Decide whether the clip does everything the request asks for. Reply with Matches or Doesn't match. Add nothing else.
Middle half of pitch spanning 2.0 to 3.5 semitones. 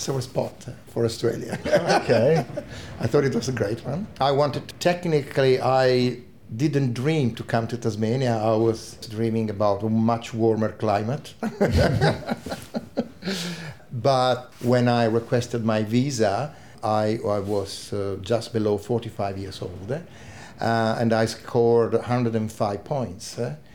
Matches